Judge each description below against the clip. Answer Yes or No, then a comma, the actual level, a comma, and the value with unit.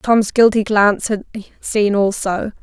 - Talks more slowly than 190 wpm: Yes, slow, 135 wpm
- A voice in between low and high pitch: No, high, 210 Hz